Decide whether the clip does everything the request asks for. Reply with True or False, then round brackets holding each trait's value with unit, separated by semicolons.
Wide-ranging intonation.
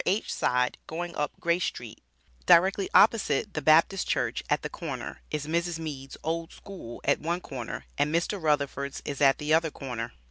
False (3.6 semitones)